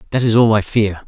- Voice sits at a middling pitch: No, low, 110 Hz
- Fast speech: Yes, fast, 280 wpm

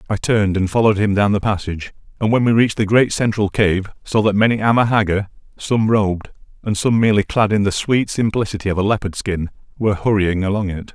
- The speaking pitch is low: Yes, low, 105 Hz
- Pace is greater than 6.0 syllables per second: Yes, 6.2 syllables/s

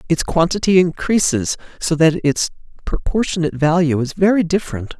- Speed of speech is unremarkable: No, slow, 130 wpm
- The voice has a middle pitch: Yes, medium, 165 Hz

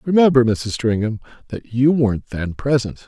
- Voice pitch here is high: No, low, 120 Hz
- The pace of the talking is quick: No, average, 155 wpm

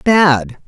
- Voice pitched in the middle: Yes, medium, 170 Hz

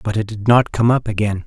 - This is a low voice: Yes, low, 110 Hz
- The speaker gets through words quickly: Yes, fast, 285 wpm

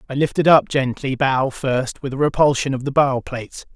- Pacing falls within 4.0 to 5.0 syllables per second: No, 5.2 syllables/s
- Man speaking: Yes, male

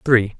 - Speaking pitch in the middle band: No, low, 115 Hz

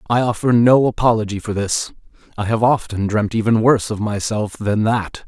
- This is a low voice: Yes, low, 110 Hz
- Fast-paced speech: No, average, 180 wpm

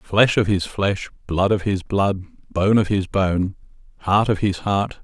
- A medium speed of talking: Yes, average, 190 wpm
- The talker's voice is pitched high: No, low, 100 Hz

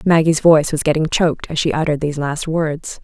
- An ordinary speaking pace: No, fast, 220 wpm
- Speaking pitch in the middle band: Yes, medium, 155 Hz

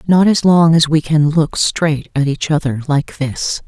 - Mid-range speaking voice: Yes, medium, 155 Hz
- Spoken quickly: Yes, fast, 210 wpm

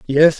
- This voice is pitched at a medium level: Yes, medium, 150 Hz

